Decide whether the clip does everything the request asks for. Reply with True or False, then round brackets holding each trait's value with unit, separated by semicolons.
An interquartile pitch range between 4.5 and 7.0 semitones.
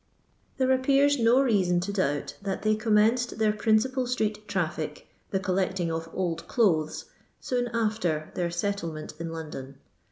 True (5.4 semitones)